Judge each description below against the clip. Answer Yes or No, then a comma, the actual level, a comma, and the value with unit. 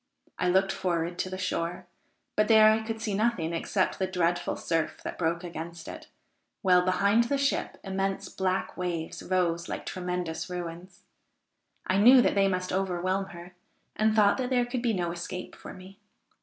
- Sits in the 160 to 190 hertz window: Yes, medium, 185 Hz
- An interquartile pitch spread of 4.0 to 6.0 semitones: No, narrow, 2.6 semitones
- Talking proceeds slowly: No, average, 175 wpm